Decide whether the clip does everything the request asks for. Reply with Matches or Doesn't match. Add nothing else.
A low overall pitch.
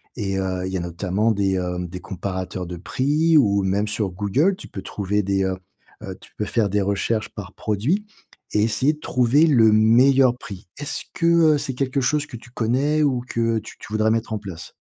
Matches